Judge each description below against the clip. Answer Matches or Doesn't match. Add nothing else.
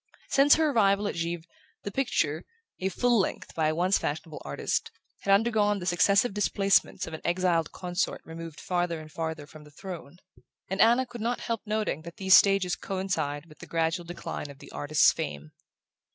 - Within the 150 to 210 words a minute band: Matches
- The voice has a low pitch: Doesn't match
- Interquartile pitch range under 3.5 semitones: Doesn't match